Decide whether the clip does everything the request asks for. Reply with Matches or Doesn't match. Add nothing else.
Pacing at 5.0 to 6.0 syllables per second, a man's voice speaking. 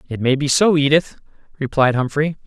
Matches